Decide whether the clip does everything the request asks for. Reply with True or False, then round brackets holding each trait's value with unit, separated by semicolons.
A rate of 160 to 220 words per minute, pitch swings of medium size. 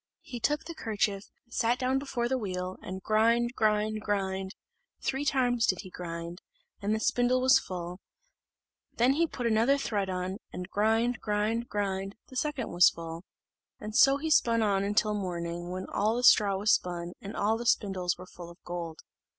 True (175 wpm; 4.4 semitones)